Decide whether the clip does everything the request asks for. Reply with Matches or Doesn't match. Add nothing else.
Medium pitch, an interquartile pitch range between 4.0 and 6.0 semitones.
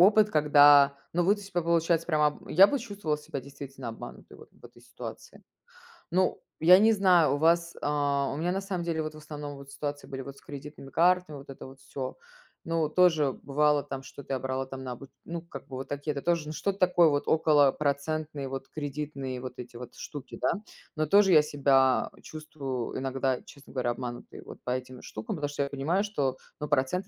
Doesn't match